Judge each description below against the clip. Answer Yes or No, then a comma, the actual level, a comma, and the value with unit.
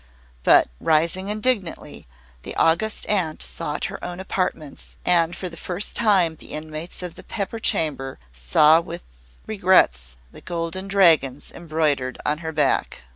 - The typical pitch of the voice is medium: Yes, medium, 165 Hz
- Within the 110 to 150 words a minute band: Yes, average, 140 wpm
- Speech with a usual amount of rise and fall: Yes, average, 3.6 semitones